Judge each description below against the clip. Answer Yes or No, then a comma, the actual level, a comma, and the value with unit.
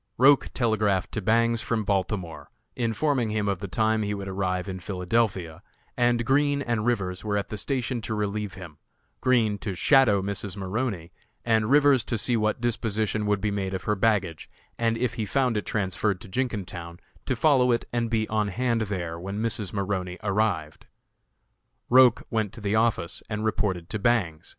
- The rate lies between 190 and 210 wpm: No, average, 180 wpm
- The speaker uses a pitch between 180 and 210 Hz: No, low, 105 Hz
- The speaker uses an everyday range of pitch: Yes, average, 3.3 semitones